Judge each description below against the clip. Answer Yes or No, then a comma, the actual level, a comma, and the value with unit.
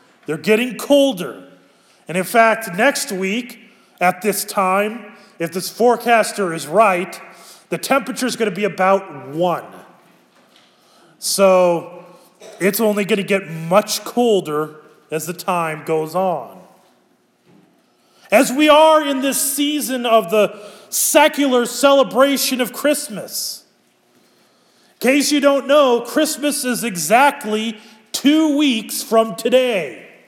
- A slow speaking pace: Yes, slow, 120 wpm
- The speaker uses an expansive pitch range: Yes, wide, 5.8 semitones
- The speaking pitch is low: No, high, 220 Hz